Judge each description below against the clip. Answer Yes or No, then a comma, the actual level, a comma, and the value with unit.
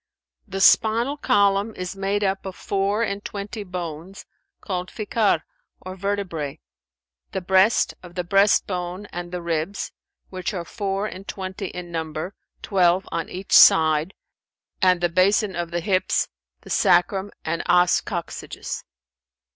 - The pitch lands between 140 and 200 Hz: Yes, high, 190 Hz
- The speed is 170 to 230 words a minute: No, average, 140 wpm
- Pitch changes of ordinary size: No, narrow, 2.3 semitones